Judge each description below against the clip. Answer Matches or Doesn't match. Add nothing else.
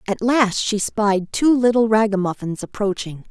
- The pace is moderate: Matches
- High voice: Matches